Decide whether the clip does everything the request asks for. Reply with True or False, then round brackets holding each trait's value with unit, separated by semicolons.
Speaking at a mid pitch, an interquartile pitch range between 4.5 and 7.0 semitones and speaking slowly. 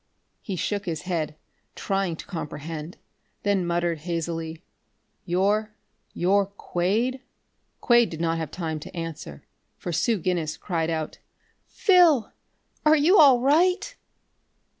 True (180 Hz; 4.9 semitones; 120 wpm)